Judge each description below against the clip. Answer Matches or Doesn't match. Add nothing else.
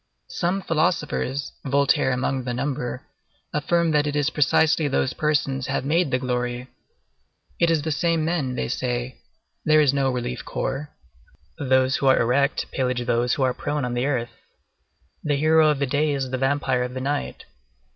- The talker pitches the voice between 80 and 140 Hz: Matches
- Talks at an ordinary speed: Matches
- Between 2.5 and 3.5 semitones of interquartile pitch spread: Matches